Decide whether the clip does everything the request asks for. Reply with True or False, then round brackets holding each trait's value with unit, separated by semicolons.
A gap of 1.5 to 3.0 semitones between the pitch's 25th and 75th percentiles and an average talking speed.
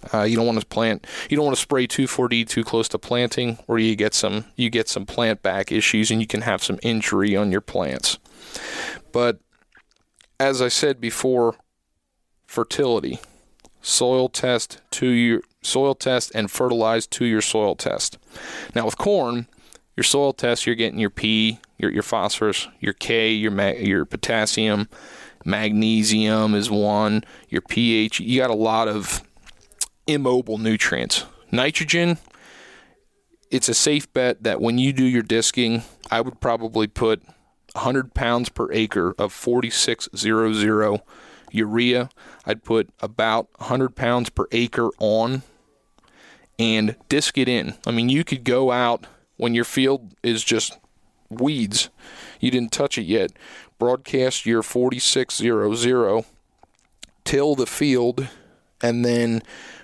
True (2.5 semitones; 145 wpm)